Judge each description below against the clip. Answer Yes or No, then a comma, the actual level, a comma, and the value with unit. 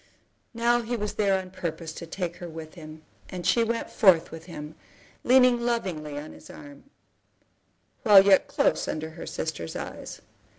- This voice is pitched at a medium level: Yes, medium, 180 Hz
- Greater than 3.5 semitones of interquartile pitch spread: Yes, wide, 5.4 semitones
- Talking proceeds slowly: No, average, 165 wpm